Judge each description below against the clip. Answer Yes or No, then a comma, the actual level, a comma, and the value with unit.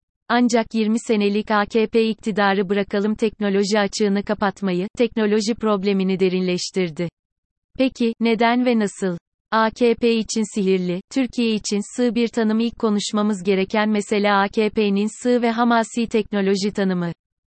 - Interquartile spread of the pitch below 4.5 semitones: Yes, narrow, 2.4 semitones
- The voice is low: No, high, 210 Hz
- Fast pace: No, average, 115 wpm